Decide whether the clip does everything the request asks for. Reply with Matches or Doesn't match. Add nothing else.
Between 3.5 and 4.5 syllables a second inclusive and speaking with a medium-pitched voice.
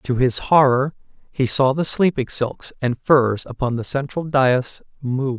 Doesn't match